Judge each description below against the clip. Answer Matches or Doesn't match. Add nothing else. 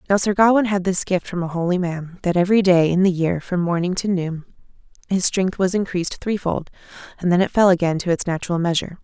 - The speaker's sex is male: Doesn't match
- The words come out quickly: Matches